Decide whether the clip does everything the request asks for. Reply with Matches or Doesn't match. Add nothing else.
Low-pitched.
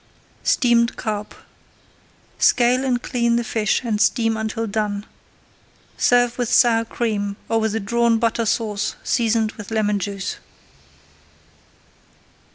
Doesn't match